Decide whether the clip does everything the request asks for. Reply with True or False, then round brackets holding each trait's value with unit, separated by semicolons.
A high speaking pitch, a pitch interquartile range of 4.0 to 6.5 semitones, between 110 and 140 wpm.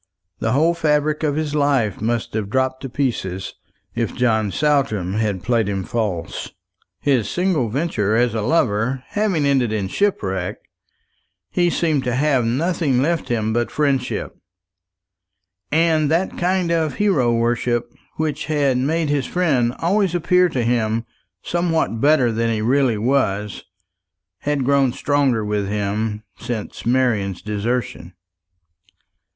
False (125 Hz; 5.6 semitones; 135 wpm)